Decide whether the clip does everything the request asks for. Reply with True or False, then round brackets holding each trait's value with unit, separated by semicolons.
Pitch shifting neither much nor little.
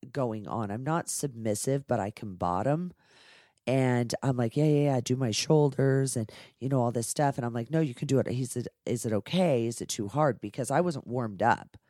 True (3.6 semitones)